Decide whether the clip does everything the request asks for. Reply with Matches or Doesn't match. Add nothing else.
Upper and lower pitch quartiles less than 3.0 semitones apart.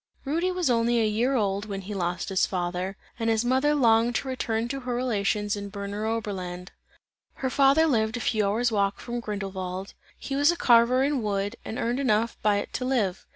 Doesn't match